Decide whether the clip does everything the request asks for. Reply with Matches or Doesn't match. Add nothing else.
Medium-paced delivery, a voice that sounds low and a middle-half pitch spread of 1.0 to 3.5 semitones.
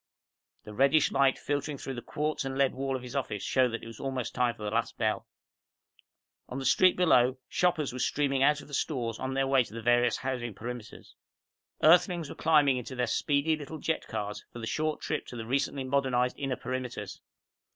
Doesn't match